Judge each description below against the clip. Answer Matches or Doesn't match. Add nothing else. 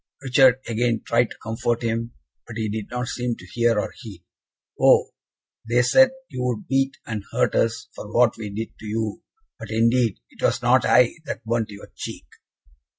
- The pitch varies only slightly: Matches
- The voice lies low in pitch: Matches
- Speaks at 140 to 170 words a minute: Doesn't match